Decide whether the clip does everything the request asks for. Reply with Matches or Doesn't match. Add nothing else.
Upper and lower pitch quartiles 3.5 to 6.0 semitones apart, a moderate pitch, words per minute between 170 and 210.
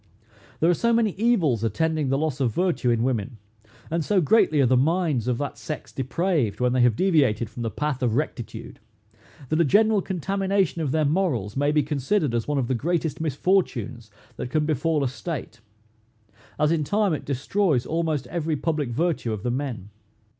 Matches